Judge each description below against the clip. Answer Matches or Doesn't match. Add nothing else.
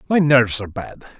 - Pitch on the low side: Matches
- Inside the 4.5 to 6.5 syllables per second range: Doesn't match